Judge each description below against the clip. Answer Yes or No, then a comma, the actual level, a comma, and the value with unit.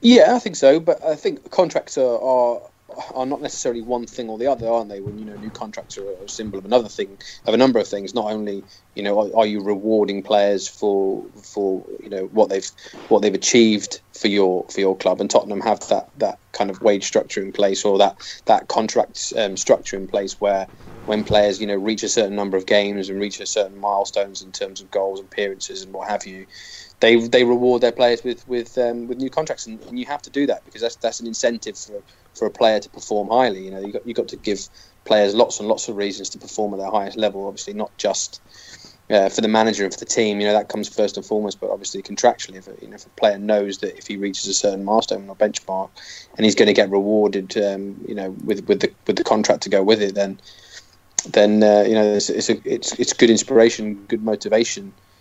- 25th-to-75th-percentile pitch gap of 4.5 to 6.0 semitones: No, average, 2.8 semitones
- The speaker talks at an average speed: No, fast, 240 wpm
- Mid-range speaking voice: No, low, 105 Hz